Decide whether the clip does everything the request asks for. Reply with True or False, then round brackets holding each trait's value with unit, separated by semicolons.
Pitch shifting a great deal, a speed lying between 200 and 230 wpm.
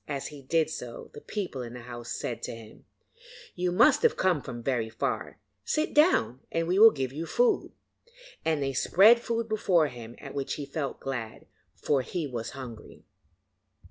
False (6.7 semitones; 175 wpm)